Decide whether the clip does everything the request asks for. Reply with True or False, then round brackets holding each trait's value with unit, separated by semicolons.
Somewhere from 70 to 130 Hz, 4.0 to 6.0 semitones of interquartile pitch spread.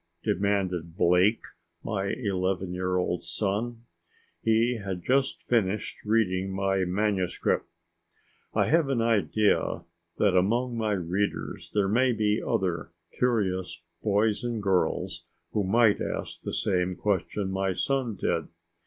False (100 Hz; 3.3 semitones)